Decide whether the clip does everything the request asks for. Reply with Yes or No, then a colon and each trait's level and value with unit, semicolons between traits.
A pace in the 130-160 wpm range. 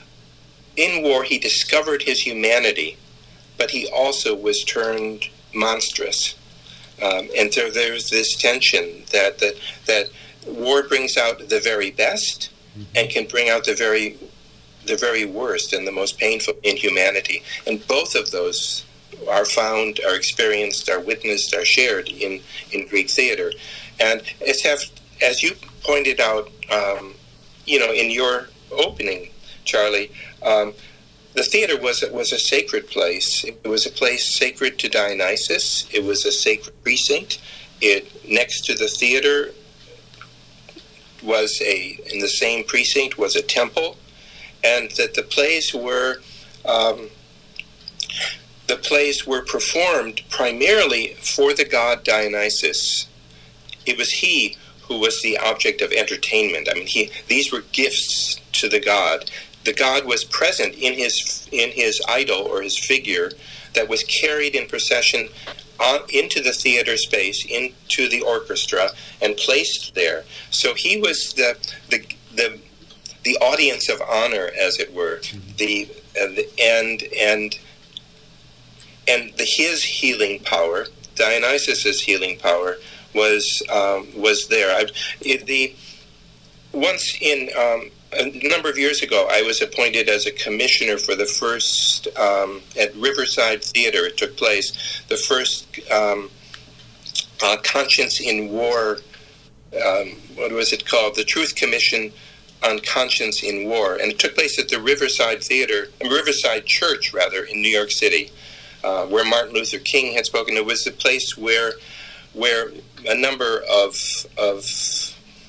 Yes: average, 140 wpm